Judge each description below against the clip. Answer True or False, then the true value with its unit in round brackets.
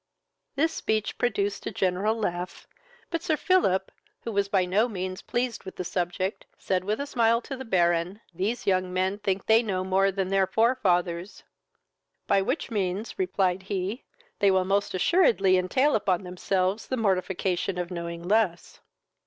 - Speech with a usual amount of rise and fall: True (3.3 semitones)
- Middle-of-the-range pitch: False (195 Hz)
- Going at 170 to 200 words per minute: False (160 wpm)